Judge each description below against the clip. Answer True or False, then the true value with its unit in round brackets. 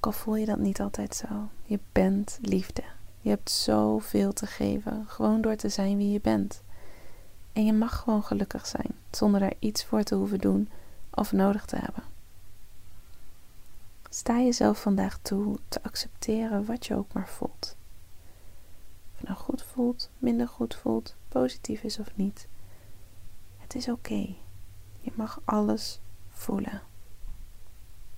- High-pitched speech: False (105 Hz)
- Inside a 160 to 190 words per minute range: False (150 wpm)